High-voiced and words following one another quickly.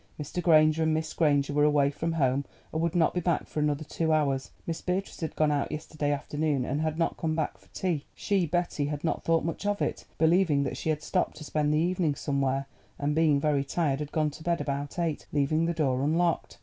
No: medium, 155 Hz; fast, 230 wpm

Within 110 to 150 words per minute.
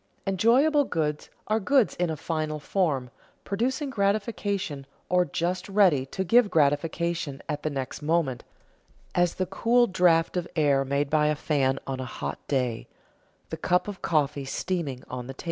No: average, 160 wpm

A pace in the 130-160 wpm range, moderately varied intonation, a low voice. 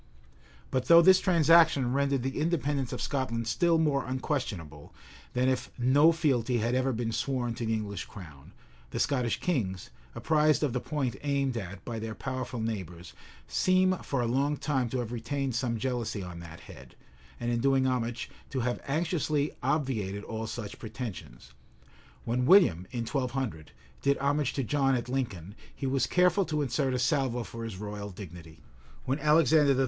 No: average, 170 wpm; average, 3.9 semitones; low, 130 Hz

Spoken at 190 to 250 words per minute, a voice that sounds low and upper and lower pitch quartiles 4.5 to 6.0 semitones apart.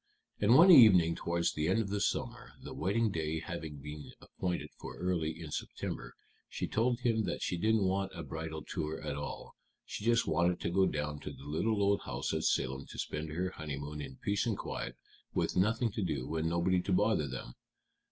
Yes: average, 200 wpm; very low, 85 Hz; average, 4.8 semitones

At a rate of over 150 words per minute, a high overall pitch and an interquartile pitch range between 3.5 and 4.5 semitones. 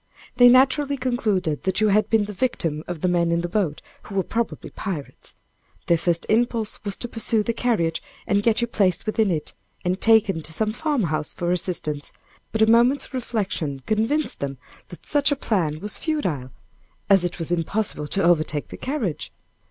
No: average, 185 wpm; high, 200 Hz; wide, 5.5 semitones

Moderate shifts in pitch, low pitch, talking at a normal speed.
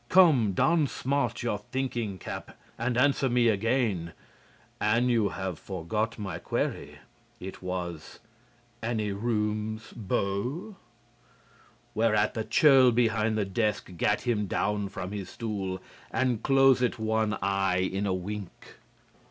No: average, 3.6 semitones; low, 110 Hz; slow, 125 wpm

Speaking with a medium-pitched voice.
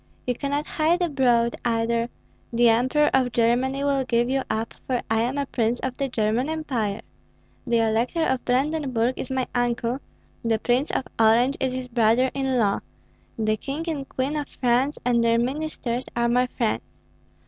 No: very high, 250 Hz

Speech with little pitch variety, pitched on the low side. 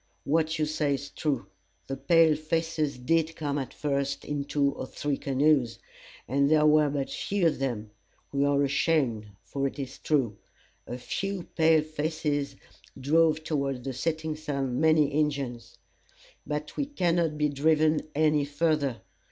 No: narrow, 2.3 semitones; medium, 150 Hz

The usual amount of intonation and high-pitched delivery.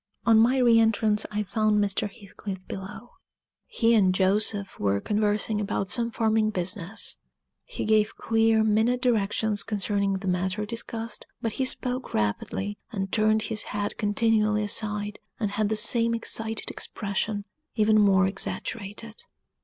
No: narrow, 1.9 semitones; high, 210 Hz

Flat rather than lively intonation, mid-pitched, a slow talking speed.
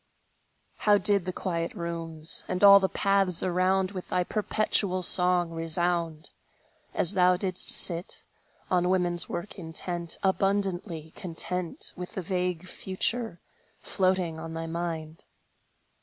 Yes: narrow, 2.1 semitones; medium, 180 Hz; slow, 125 wpm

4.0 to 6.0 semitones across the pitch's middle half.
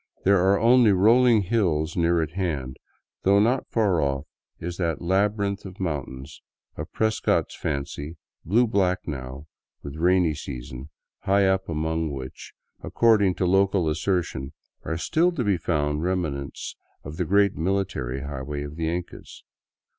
Yes: average, 5.0 semitones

